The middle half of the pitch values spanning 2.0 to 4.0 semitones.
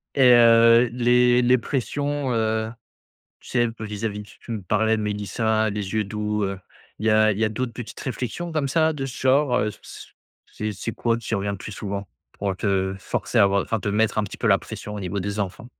Yes: average, 2.9 semitones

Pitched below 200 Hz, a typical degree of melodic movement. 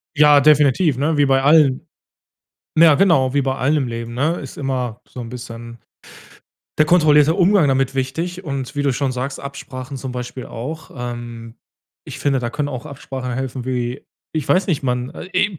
Yes: low, 135 Hz; average, 3.2 semitones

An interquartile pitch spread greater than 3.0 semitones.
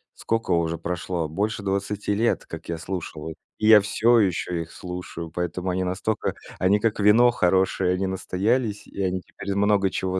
No: average, 2.7 semitones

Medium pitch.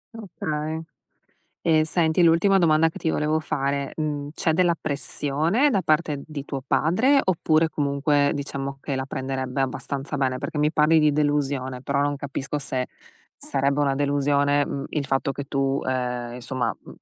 Yes: medium, 145 Hz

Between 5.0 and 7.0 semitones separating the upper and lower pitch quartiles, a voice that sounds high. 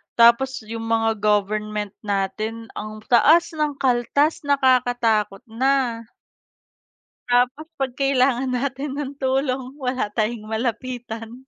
No: average, 3.3 semitones; high, 245 Hz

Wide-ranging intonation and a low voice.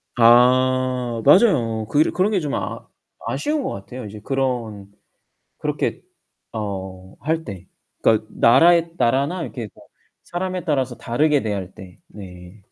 Yes: wide, 6.2 semitones; low, 125 Hz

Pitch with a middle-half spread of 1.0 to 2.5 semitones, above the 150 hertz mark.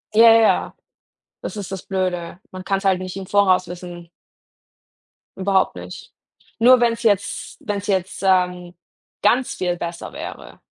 Yes: narrow, 2.2 semitones; high, 190 Hz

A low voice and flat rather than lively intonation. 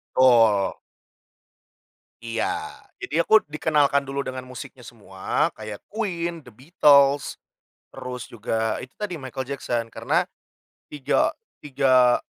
No: low, 130 Hz; average, 3.7 semitones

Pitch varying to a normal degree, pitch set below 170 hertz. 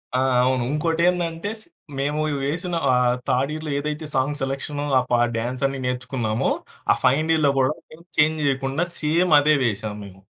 Yes: average, 3.6 semitones; medium, 140 Hz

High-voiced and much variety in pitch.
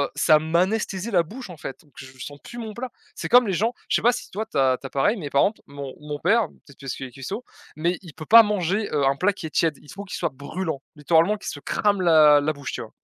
No: medium, 165 Hz; wide, 6.3 semitones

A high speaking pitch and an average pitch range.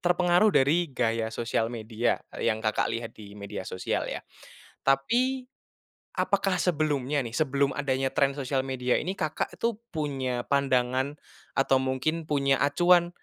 No: low, 135 Hz; average, 4.5 semitones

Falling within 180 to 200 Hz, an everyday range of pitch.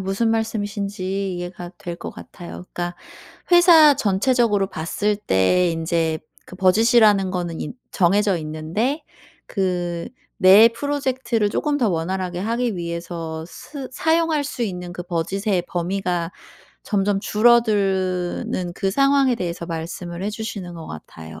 Yes: high, 190 Hz; average, 4.3 semitones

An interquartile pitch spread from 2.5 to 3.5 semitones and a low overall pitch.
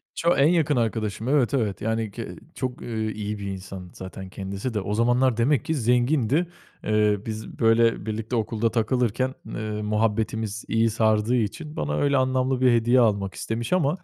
Yes: average, 3.2 semitones; low, 115 Hz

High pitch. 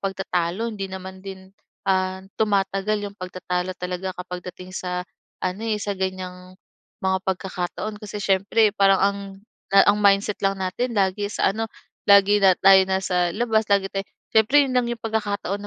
Yes: high, 195 Hz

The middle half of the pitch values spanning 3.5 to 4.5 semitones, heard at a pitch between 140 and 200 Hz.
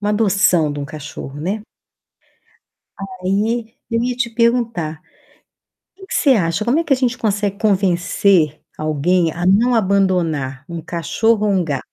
No: wide, 5.5 semitones; high, 195 Hz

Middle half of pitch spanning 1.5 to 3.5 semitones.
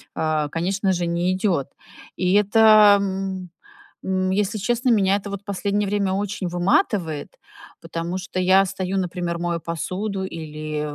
Yes: narrow, 2.6 semitones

